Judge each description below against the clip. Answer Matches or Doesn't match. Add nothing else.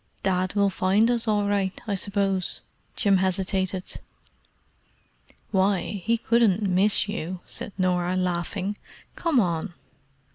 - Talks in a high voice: Matches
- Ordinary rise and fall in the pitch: Doesn't match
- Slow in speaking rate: Matches